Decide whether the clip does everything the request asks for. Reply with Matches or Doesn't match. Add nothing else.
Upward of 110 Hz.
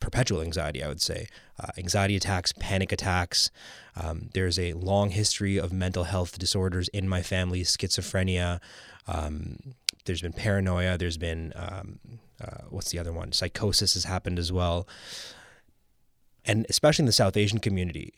Doesn't match